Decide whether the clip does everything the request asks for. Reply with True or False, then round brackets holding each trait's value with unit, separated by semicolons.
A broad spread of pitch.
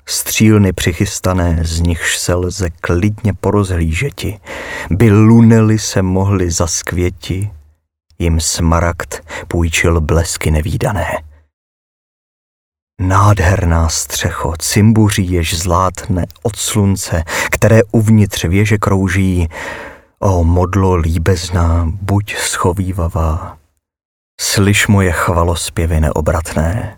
False (3.2 semitones)